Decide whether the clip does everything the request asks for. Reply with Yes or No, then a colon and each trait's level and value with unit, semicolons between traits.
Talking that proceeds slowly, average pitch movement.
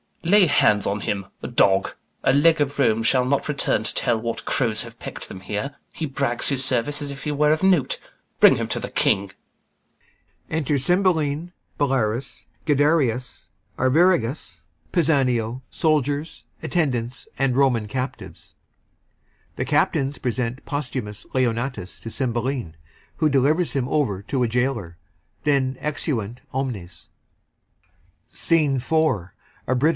Yes: slow, 125 wpm; average, 4.1 semitones